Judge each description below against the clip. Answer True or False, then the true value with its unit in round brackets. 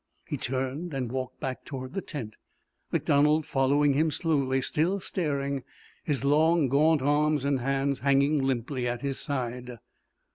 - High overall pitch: False (140 Hz)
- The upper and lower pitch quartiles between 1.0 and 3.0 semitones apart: True (2.5 semitones)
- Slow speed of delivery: False (145 wpm)